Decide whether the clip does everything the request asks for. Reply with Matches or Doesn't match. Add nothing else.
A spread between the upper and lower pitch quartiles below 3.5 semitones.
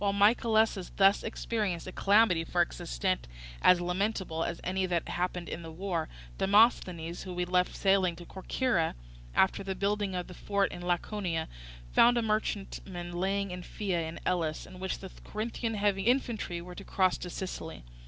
Matches